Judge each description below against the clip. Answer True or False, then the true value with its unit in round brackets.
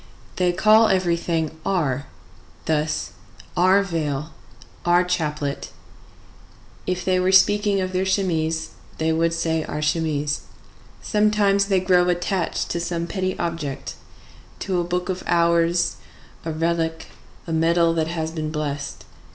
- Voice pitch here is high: False (170 Hz)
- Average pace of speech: False (125 wpm)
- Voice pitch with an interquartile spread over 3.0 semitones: False (2.5 semitones)